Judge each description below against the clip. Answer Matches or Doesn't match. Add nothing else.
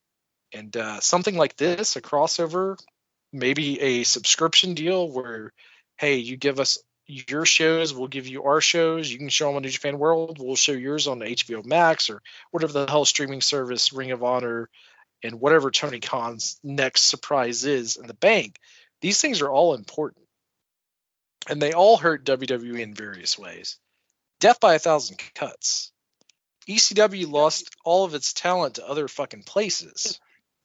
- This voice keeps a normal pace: Matches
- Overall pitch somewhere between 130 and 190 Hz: Matches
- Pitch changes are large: Doesn't match